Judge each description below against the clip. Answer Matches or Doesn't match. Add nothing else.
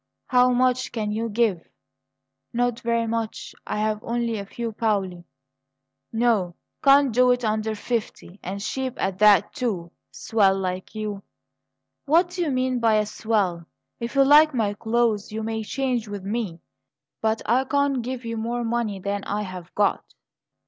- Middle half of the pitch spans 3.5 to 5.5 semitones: Doesn't match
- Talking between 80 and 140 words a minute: Doesn't match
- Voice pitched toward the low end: Doesn't match